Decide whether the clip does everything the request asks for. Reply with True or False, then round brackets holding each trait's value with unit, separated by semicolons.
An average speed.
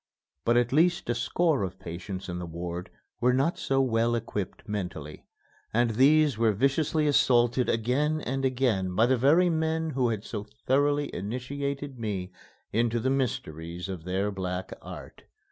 True (160 wpm)